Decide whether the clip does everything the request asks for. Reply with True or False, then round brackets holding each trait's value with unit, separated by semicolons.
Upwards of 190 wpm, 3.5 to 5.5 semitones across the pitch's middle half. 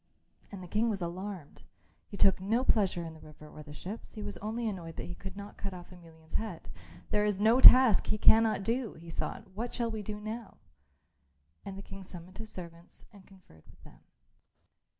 True (205 wpm; 3.8 semitones)